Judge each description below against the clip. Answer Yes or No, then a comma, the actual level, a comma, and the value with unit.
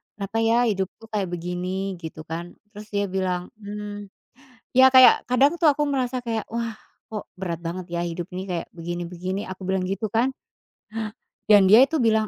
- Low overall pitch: No, high, 200 Hz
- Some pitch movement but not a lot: Yes, average, 4.0 semitones